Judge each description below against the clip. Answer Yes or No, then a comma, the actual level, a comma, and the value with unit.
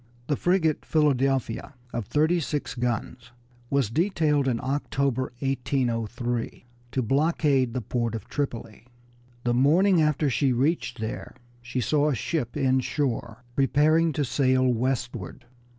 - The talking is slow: Yes, slow, 125 wpm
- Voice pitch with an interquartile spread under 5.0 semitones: Yes, average, 3.6 semitones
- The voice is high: No, low, 135 Hz